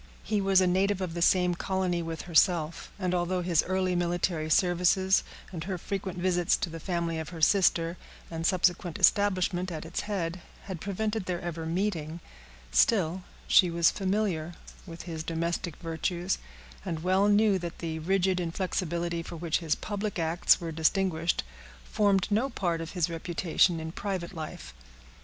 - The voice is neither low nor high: Yes, medium, 175 Hz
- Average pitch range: No, narrow, 2.3 semitones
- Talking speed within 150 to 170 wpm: Yes, average, 160 wpm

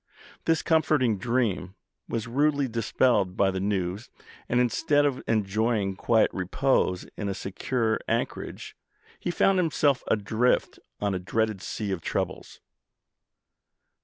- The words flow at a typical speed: No, slow, 125 wpm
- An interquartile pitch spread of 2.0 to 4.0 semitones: No, average, 5.0 semitones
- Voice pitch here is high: No, low, 110 Hz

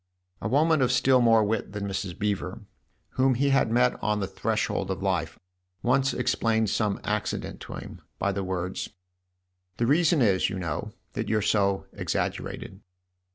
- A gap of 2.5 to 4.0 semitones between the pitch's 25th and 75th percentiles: No, average, 4.6 semitones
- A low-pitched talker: Yes, low, 105 Hz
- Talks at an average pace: Yes, average, 165 wpm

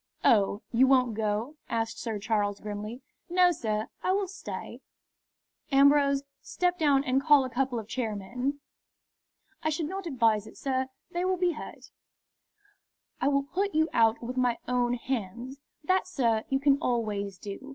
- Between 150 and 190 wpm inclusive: Yes, average, 160 wpm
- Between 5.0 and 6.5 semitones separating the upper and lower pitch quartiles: No, average, 4.6 semitones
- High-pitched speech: Yes, very high, 255 Hz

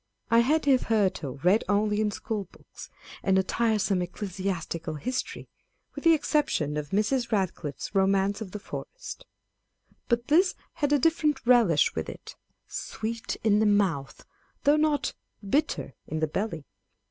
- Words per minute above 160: No, average, 155 wpm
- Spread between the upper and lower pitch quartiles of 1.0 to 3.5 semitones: No, average, 5.1 semitones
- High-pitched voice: Yes, high, 210 Hz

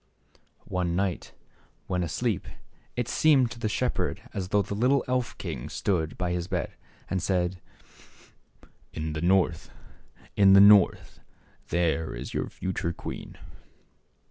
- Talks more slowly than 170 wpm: Yes, average, 145 wpm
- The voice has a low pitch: Yes, very low, 95 Hz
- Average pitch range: Yes, average, 3.2 semitones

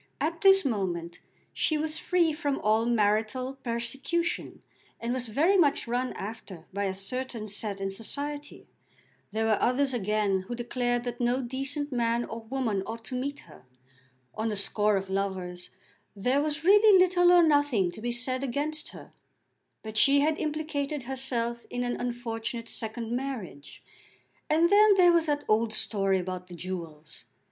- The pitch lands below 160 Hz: No, high, 240 Hz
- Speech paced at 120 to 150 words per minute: No, average, 160 wpm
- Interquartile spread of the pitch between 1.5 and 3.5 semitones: No, average, 5.3 semitones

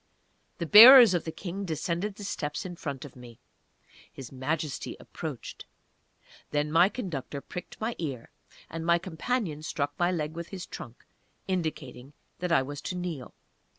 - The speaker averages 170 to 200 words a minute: No, average, 155 wpm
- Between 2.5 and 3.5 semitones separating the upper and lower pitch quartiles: No, average, 4.0 semitones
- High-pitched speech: No, medium, 165 Hz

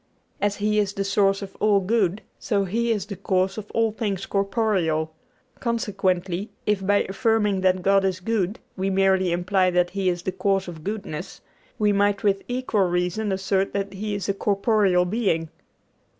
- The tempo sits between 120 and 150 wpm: No, average, 175 wpm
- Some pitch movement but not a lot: No, narrow, 2.0 semitones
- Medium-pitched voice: No, high, 195 Hz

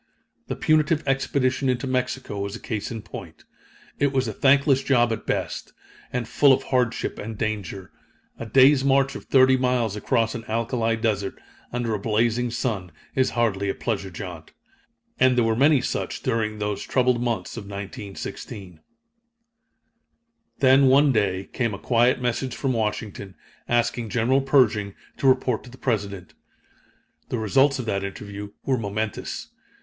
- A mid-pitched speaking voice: No, low, 115 Hz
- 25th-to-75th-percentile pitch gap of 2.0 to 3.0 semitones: No, average, 3.9 semitones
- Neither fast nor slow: Yes, average, 155 wpm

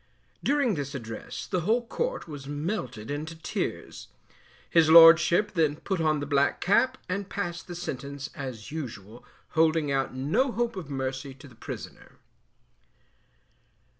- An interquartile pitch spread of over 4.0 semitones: Yes, average, 4.9 semitones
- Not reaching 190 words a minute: Yes, average, 140 wpm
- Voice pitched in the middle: Yes, medium, 155 Hz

